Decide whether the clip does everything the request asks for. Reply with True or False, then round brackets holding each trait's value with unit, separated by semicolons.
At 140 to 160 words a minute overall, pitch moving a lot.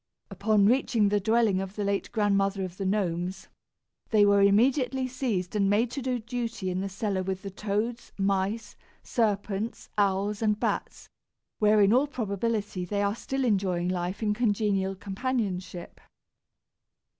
False (150 wpm; 2.8 semitones)